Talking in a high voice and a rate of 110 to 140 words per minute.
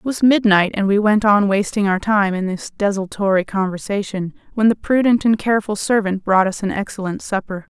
No: high, 205 Hz; average, 195 wpm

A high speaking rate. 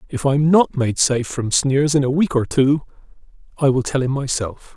Yes: fast, 225 wpm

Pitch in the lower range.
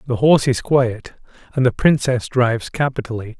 Yes: low, 125 Hz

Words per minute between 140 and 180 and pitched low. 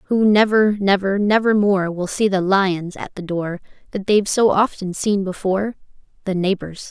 No: average, 165 wpm; high, 195 Hz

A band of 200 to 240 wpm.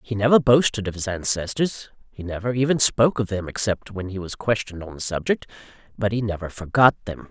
Yes: fast, 205 wpm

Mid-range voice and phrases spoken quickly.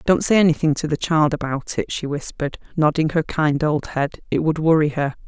Yes: medium, 150 Hz; fast, 215 wpm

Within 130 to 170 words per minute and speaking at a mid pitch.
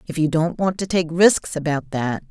No: fast, 235 wpm; medium, 165 Hz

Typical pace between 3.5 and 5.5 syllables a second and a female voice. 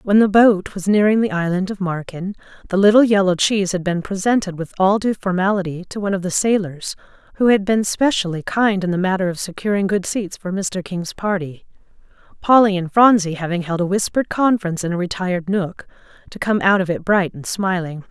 No: 5.7 syllables/s; female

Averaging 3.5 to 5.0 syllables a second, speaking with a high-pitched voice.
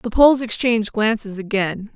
No: 5.3 syllables/s; high, 220 Hz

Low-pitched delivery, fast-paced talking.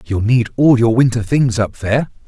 Yes: low, 115 Hz; fast, 210 wpm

